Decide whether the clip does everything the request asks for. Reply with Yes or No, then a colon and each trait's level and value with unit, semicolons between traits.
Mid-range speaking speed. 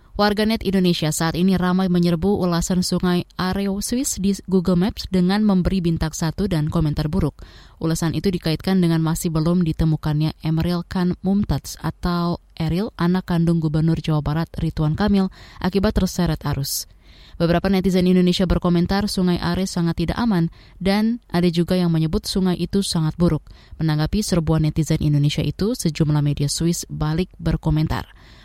No: fast, 150 wpm